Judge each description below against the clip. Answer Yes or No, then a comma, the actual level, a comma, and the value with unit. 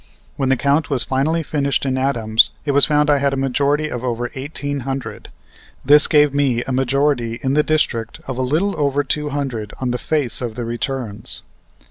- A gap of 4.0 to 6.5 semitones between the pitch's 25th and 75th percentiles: No, average, 2.8 semitones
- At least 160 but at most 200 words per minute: Yes, average, 195 wpm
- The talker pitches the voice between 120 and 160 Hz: Yes, low, 135 Hz